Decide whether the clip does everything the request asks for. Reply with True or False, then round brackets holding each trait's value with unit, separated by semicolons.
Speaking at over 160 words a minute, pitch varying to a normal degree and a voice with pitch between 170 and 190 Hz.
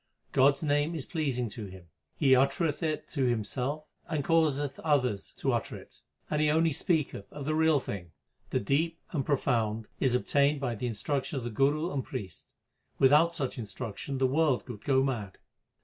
False (180 wpm; 3.9 semitones; 135 Hz)